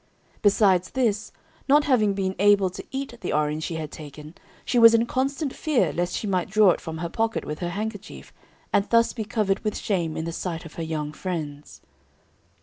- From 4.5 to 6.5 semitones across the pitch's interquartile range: Yes, wide, 5.5 semitones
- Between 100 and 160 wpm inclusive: No, average, 200 wpm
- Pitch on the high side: Yes, high, 195 Hz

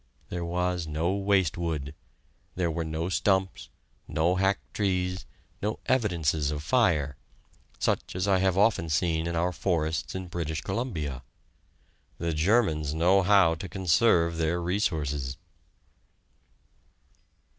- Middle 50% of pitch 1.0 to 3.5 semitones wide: Yes, average, 3.2 semitones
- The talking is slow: Yes, slow, 125 wpm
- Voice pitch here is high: No, very low, 85 Hz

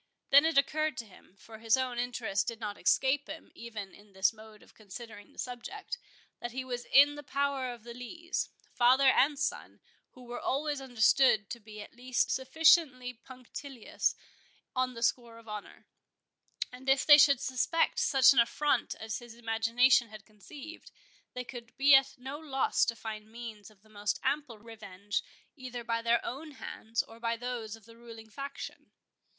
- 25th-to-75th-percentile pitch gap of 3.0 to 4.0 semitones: Yes, average, 3.3 semitones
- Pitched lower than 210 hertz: No, high, 245 Hz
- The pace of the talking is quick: No, average, 175 wpm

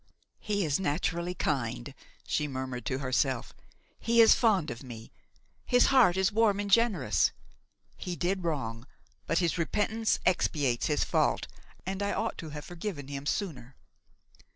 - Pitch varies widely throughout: Yes, wide, 7.0 semitones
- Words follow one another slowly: No, average, 150 wpm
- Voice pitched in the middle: Yes, medium, 165 Hz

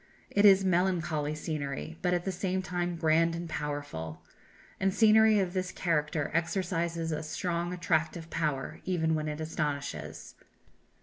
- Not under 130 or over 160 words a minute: Yes, average, 140 wpm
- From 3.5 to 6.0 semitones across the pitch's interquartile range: No, average, 2.9 semitones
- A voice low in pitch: No, medium, 165 Hz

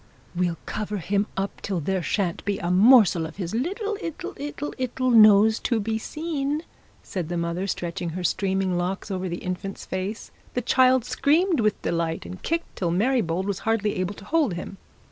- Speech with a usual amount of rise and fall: No, wide, 5.7 semitones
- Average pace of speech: Yes, average, 185 wpm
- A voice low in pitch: No, high, 200 Hz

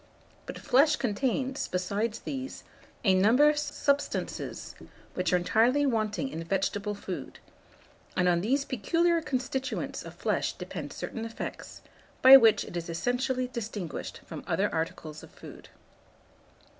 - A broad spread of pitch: Yes, wide, 5.7 semitones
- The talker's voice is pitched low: No, high, 230 Hz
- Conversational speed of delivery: No, slow, 130 wpm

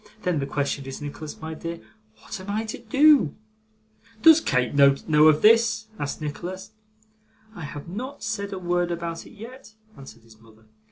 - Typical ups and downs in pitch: No, wide, 6.9 semitones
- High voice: No, medium, 170 Hz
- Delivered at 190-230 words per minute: No, average, 170 wpm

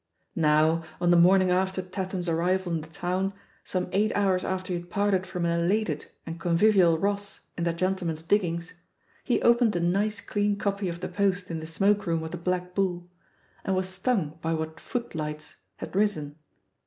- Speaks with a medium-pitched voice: Yes, medium, 180 Hz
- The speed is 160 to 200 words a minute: Yes, average, 190 wpm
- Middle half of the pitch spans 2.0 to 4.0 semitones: Yes, average, 2.8 semitones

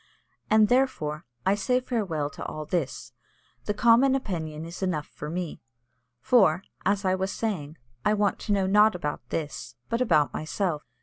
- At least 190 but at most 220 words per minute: No, average, 165 wpm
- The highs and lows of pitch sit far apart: Yes, wide, 5.7 semitones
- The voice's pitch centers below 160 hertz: No, high, 190 Hz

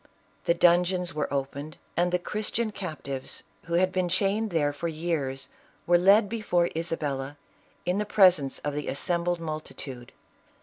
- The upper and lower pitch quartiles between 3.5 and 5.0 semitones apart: Yes, average, 3.9 semitones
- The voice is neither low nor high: Yes, medium, 170 Hz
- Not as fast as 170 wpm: Yes, average, 160 wpm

